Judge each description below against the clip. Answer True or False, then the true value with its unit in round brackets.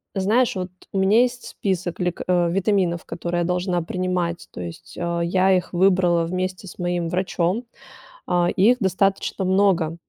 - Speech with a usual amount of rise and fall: False (1.9 semitones)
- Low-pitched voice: False (180 Hz)